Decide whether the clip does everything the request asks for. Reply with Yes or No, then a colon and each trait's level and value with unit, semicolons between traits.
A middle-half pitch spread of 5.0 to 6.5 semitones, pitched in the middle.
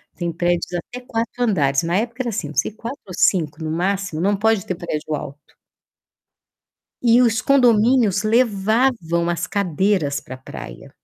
No: average, 5.3 semitones; high, 195 Hz